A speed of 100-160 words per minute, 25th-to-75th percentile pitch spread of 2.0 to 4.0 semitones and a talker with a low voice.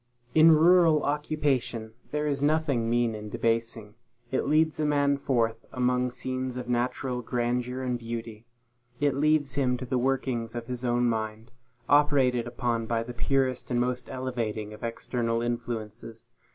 Yes: average, 150 wpm; average, 2.9 semitones; low, 125 Hz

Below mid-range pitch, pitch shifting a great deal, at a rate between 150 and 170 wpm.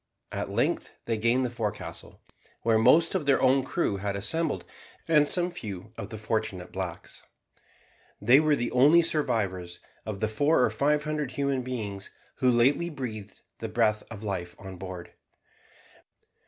Yes: low, 115 Hz; wide, 5.9 semitones; average, 155 wpm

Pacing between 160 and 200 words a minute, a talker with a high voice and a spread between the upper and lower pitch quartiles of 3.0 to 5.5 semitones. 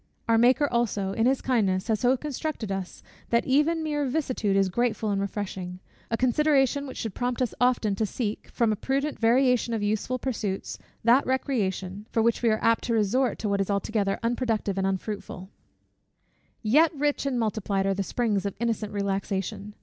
Yes: average, 180 wpm; high, 225 Hz; average, 4.2 semitones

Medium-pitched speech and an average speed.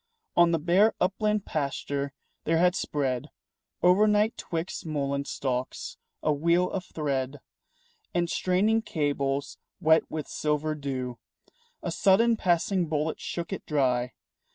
No: medium, 160 Hz; slow, 125 wpm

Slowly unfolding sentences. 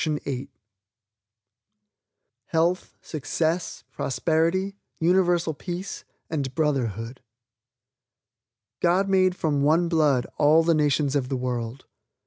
Yes: slow, 90 wpm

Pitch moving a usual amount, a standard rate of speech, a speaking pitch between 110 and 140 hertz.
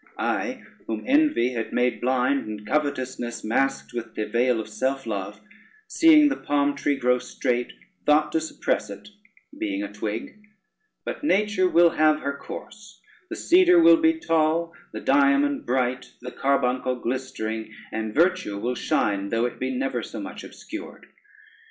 No: wide, 5.9 semitones; average, 155 wpm; low, 135 Hz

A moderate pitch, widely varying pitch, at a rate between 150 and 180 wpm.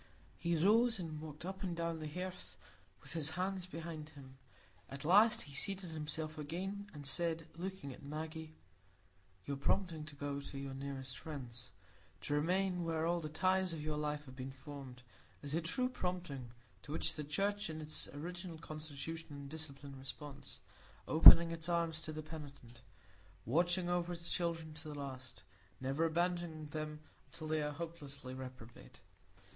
No: medium, 155 Hz; average, 3.3 semitones; average, 160 wpm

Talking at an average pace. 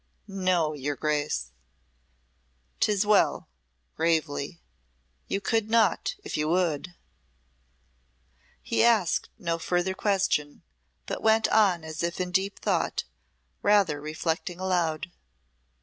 No: slow, 105 wpm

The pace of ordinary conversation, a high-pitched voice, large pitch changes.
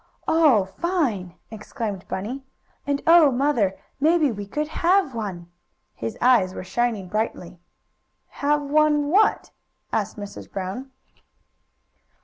No: slow, 115 wpm; high, 240 Hz; wide, 7.1 semitones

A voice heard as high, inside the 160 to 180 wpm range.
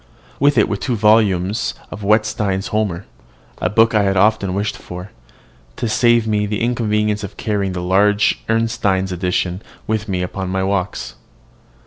No: low, 105 Hz; average, 165 wpm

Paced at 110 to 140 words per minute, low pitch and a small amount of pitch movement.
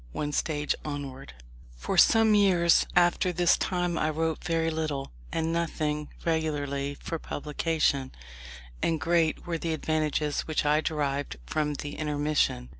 No: slow, 135 wpm; medium, 155 Hz; narrow, 2.2 semitones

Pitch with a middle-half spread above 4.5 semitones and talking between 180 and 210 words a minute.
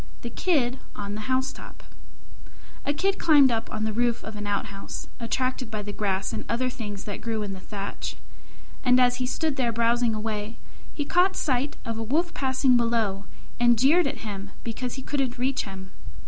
No: average, 3.6 semitones; average, 190 wpm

